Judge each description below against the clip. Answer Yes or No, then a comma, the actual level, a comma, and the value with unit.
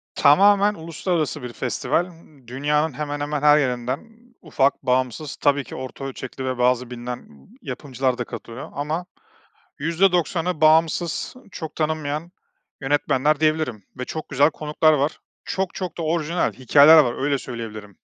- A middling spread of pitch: Yes, average, 3.7 semitones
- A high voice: No, medium, 145 Hz